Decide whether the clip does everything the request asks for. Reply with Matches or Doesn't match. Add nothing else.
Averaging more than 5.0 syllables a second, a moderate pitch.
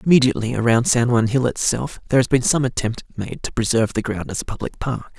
Doesn't match